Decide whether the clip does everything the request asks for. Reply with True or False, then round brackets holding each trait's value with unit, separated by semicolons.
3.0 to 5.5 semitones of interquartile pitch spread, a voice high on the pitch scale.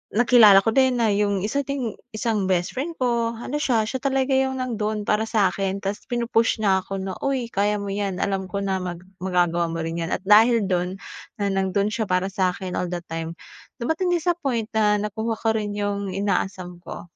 True (3.7 semitones; 205 Hz)